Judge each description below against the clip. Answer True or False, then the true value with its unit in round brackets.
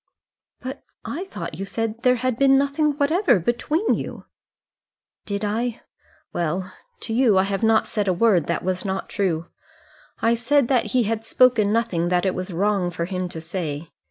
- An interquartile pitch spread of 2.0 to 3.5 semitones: False (5.3 semitones)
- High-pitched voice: True (215 Hz)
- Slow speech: False (180 wpm)